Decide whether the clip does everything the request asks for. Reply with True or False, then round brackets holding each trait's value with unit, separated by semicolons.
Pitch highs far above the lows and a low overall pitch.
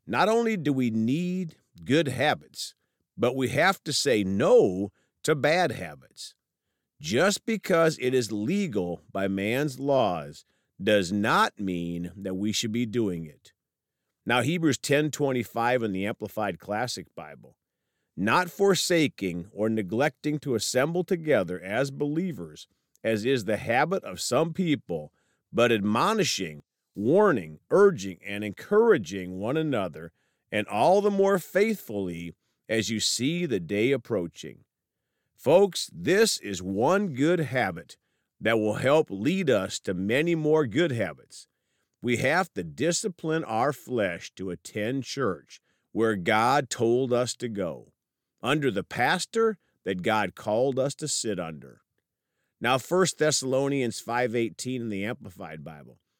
True (7.6 semitones; 125 Hz)